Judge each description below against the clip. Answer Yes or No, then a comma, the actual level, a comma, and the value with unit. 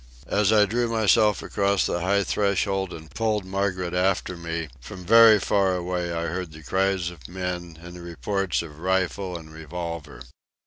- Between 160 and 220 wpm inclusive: Yes, average, 170 wpm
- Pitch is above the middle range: No, very low, 90 Hz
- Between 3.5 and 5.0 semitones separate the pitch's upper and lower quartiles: No, average, 2.8 semitones